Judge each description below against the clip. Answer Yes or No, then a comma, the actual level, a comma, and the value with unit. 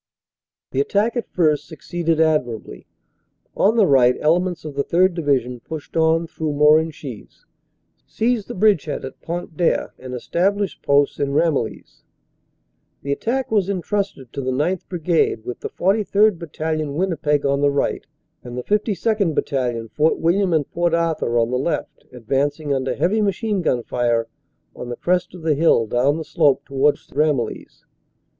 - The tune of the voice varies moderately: Yes, average, 4.6 semitones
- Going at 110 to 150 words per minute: No, average, 160 wpm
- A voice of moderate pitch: Yes, medium, 155 Hz